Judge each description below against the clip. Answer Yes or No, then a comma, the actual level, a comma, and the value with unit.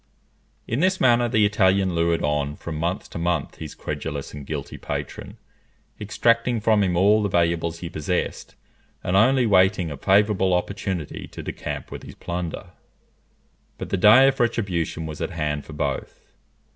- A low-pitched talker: Yes, very low, 90 Hz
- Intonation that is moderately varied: Yes, average, 4.3 semitones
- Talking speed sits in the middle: Yes, average, 160 wpm